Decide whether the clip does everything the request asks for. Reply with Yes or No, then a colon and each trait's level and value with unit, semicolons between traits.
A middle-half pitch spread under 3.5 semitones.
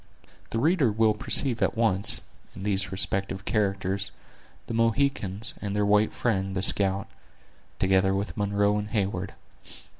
Yes: narrow, 2.5 semitones